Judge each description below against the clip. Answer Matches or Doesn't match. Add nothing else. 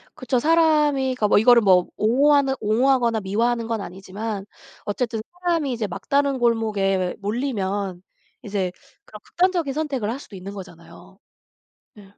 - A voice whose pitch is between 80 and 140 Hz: Doesn't match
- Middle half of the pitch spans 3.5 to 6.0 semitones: Matches